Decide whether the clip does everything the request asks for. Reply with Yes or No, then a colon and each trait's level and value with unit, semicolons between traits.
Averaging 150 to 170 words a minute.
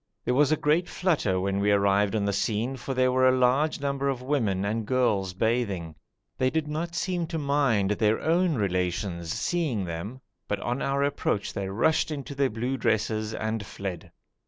No: average, 185 wpm